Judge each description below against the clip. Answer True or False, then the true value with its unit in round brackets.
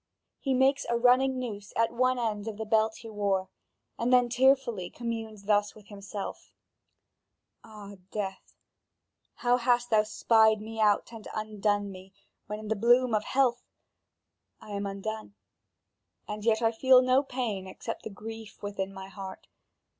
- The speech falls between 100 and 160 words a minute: True (155 wpm)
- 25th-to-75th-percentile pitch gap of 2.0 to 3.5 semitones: True (2.9 semitones)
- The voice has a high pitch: True (220 Hz)